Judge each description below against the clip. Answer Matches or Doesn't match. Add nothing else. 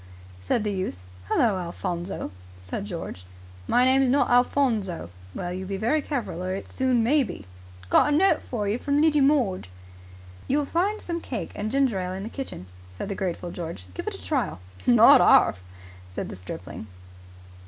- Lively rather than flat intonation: Matches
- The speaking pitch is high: Matches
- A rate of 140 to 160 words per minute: Doesn't match